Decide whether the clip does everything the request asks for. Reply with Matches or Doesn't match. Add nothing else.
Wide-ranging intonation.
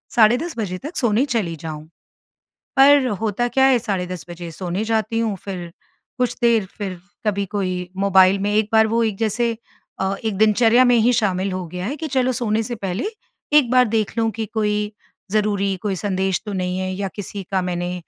Doesn't match